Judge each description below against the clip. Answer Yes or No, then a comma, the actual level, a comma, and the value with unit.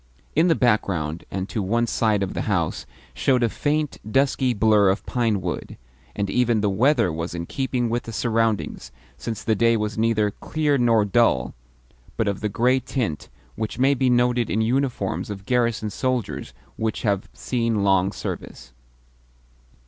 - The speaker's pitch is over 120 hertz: No, low, 110 Hz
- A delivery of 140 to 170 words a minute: Yes, average, 165 wpm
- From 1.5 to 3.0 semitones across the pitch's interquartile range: No, average, 3.6 semitones